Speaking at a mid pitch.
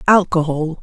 Yes: medium, 170 Hz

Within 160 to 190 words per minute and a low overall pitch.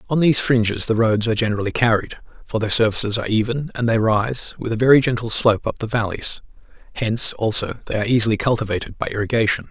No: average, 200 wpm; low, 115 Hz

